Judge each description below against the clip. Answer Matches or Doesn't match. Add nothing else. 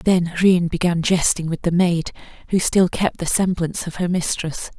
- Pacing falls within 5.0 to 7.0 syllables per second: Doesn't match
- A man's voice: Doesn't match